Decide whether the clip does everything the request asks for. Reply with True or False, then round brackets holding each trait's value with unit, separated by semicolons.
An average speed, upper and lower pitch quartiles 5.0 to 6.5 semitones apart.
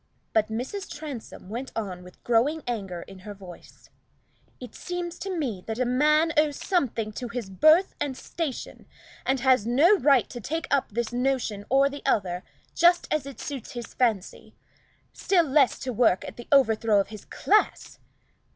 True (170 wpm; 5.4 semitones)